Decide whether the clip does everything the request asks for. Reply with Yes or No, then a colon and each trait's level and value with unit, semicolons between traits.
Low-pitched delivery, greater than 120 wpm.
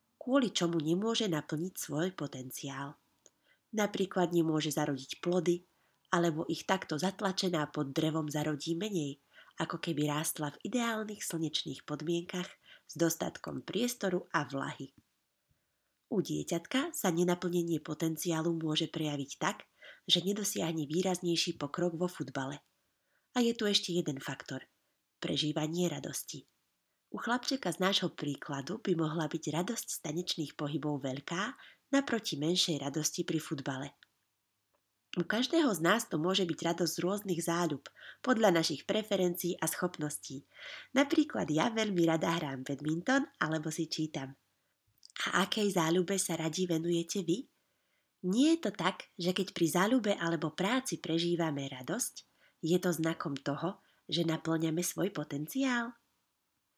No: medium, 170 Hz; average, 130 wpm